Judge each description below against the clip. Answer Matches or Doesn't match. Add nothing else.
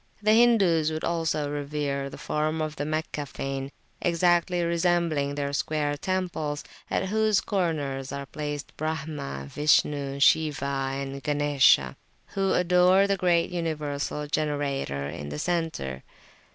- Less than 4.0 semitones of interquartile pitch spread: Matches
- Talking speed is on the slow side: Matches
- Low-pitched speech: Doesn't match